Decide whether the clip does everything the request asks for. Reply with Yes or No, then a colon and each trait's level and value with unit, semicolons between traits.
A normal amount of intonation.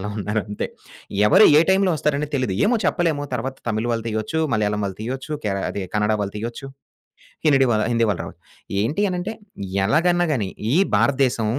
No: wide, 6.0 semitones